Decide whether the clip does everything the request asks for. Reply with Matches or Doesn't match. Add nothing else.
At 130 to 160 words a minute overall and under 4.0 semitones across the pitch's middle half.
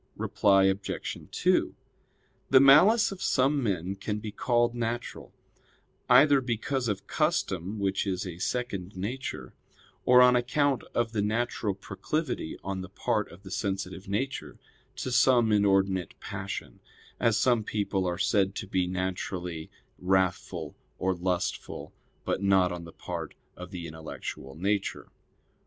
Doesn't match